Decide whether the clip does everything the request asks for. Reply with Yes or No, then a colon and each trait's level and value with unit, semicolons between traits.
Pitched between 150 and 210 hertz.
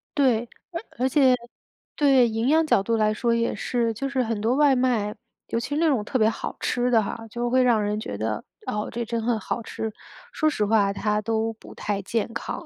No: high, 230 Hz